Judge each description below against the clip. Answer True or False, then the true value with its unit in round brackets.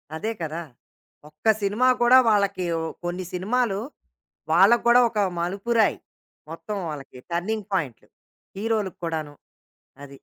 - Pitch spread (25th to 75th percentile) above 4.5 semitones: True (5.0 semitones)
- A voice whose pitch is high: True (195 Hz)